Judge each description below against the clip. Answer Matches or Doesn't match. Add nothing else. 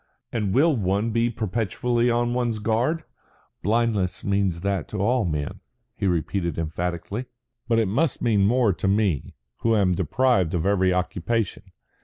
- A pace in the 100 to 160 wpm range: Matches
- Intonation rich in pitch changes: Doesn't match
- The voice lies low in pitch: Matches